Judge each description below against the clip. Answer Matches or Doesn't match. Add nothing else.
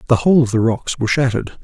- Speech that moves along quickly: Matches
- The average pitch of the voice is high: Doesn't match